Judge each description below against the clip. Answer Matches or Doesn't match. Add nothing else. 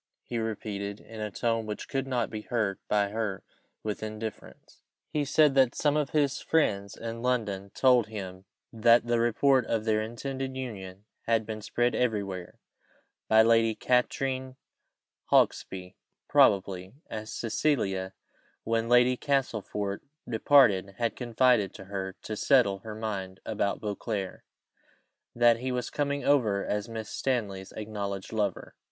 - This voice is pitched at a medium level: Doesn't match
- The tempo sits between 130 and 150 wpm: Matches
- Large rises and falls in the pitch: Doesn't match